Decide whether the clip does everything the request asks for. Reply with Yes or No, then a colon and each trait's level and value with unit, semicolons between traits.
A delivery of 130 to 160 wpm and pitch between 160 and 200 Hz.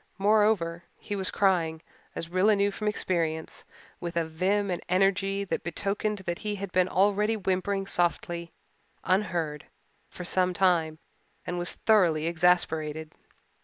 Yes: slow, 135 wpm; medium, 185 Hz